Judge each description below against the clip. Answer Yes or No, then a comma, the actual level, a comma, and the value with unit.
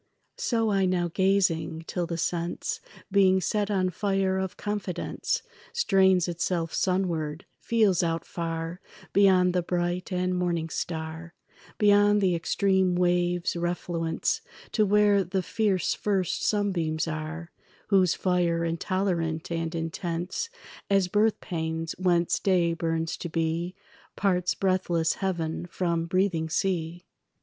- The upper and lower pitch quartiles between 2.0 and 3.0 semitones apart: Yes, narrow, 2.5 semitones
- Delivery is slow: Yes, slow, 120 wpm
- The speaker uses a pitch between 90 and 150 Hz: No, medium, 180 Hz